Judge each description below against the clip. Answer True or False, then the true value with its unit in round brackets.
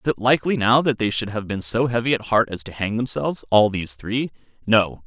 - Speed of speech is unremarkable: False (250 wpm)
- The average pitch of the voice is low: True (110 Hz)